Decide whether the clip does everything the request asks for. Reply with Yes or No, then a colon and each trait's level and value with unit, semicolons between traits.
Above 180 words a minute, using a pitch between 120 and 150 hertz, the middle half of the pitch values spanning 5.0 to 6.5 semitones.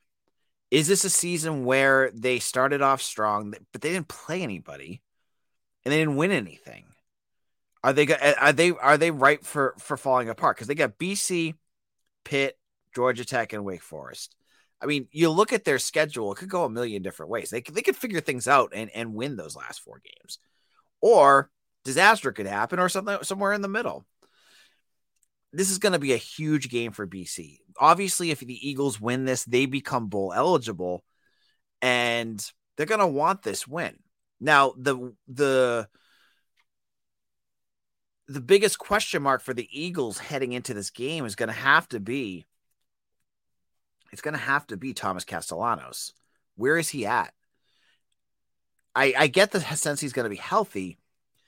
No: average, 170 wpm; medium, 140 Hz; wide, 5.4 semitones